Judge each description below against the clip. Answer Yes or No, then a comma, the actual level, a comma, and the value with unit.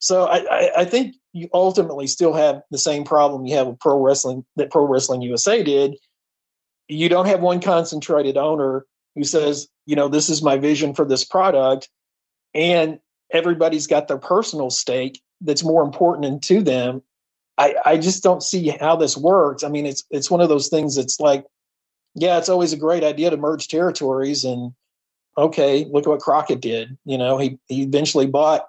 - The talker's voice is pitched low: No, medium, 150 Hz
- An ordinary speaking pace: Yes, average, 190 wpm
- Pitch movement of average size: Yes, average, 3.7 semitones